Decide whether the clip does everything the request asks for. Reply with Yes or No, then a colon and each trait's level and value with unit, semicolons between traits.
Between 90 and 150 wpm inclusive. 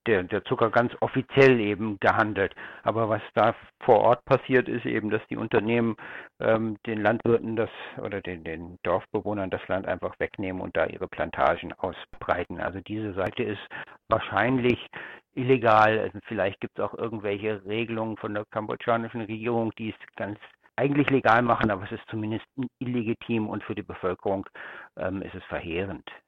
No: average, 160 wpm